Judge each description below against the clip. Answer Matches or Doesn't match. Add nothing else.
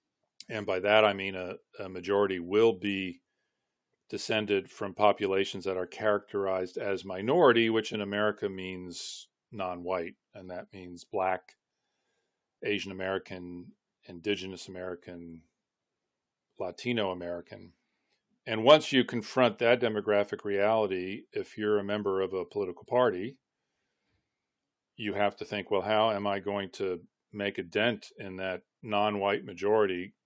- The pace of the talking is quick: Doesn't match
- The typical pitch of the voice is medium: Doesn't match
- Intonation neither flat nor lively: Doesn't match